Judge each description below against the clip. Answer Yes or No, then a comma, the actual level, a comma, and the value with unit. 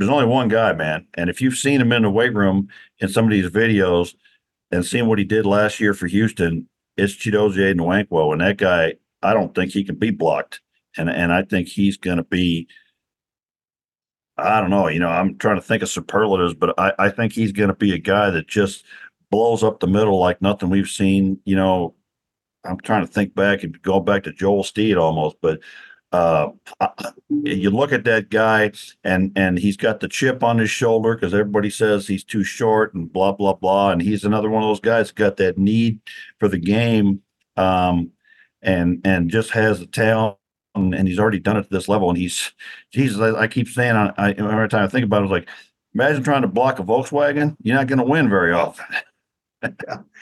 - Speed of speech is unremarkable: No, fast, 215 wpm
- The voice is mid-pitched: No, low, 100 Hz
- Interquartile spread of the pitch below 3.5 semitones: Yes, average, 2.8 semitones